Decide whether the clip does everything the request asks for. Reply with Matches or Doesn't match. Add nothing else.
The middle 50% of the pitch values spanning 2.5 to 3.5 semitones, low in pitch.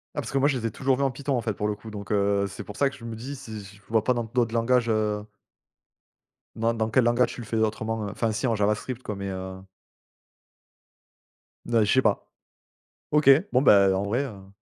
Matches